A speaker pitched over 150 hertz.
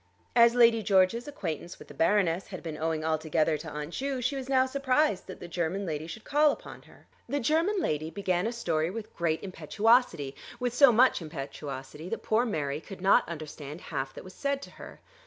Yes: medium, 185 Hz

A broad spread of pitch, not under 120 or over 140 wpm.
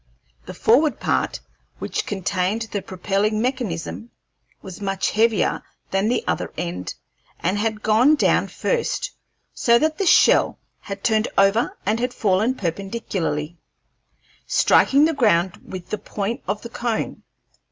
No: average, 3.8 semitones; slow, 135 wpm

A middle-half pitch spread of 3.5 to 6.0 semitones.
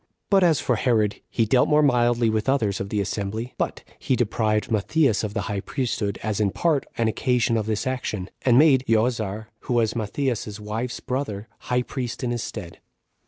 No: average, 3.1 semitones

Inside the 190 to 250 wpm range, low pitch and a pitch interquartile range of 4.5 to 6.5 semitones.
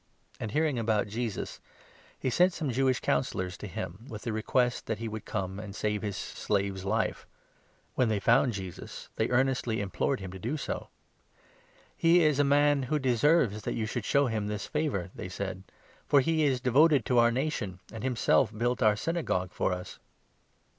Yes: average, 200 wpm; low, 115 Hz; average, 4.9 semitones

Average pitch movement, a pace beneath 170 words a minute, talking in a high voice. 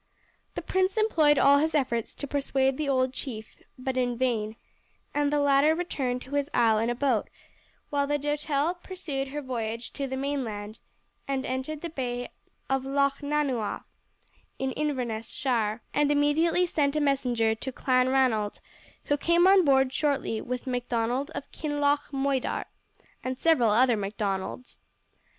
Yes: average, 3.0 semitones; average, 150 wpm; very high, 270 Hz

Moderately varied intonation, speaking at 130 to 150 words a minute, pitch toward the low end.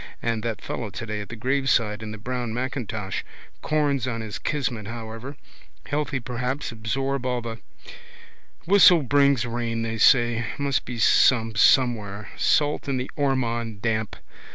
Yes: average, 3.3 semitones; average, 145 wpm; low, 120 Hz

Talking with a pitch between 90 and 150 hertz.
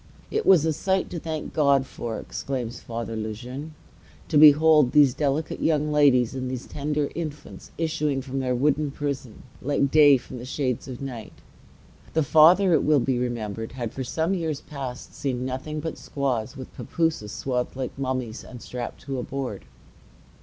Yes: low, 135 Hz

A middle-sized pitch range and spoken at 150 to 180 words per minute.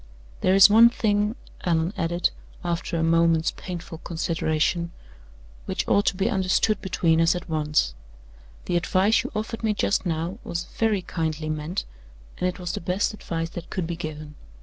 Yes: average, 3.1 semitones; average, 170 wpm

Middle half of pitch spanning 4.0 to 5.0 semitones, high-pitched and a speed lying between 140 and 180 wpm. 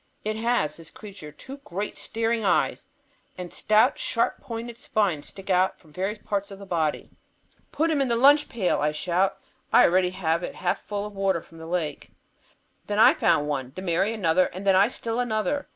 No: average, 4.6 semitones; high, 195 Hz; average, 200 wpm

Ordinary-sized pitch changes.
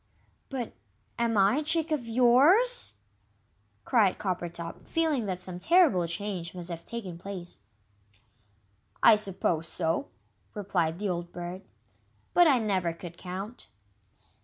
No: wide, 5.8 semitones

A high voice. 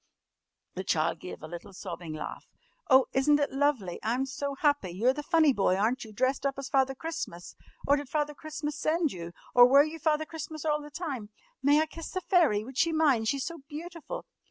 Yes: very high, 280 Hz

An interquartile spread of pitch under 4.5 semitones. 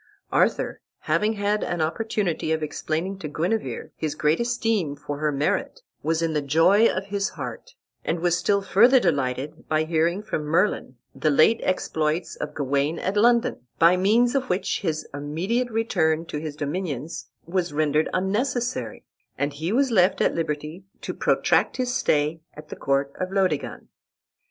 No: average, 5.1 semitones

